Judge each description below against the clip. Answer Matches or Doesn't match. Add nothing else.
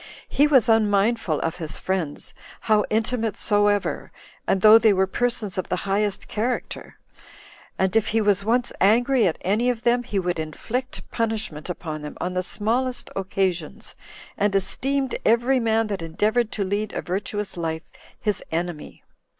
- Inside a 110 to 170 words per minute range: Matches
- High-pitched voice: Matches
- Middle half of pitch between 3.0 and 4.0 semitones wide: Matches